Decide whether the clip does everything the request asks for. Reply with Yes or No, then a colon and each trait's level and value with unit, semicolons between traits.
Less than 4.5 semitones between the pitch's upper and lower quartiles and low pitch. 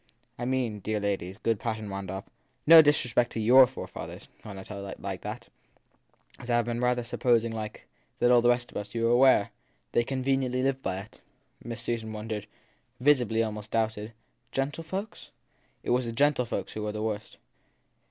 Yes: average, 2.8 semitones; low, 115 Hz